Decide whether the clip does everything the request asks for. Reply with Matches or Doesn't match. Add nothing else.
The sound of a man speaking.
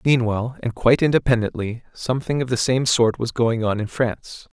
Matches